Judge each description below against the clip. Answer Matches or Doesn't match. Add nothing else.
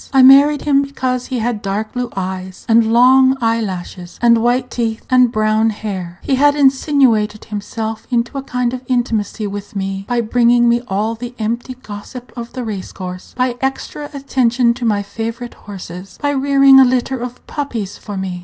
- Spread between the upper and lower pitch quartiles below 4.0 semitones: Matches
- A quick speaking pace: Doesn't match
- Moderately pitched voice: Doesn't match